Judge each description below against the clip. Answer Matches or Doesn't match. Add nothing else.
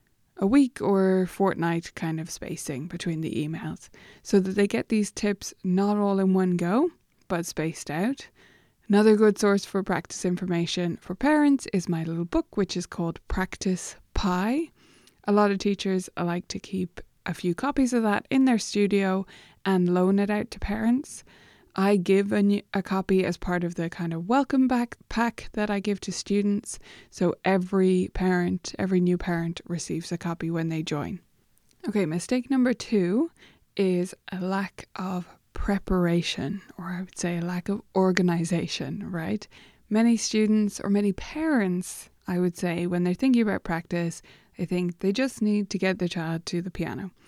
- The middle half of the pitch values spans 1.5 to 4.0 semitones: Matches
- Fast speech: Doesn't match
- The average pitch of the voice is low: Doesn't match